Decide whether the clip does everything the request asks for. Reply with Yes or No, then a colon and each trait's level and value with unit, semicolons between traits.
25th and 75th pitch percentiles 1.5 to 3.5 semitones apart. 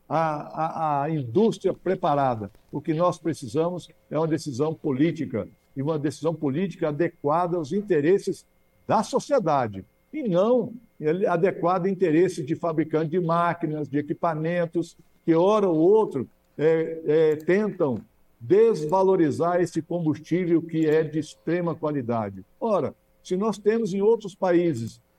Yes: average, 2.8 semitones